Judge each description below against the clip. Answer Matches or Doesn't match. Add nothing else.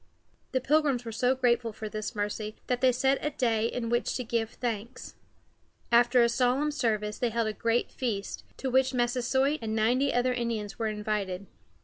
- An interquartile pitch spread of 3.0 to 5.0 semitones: Doesn't match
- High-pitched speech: Matches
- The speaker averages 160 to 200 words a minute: Matches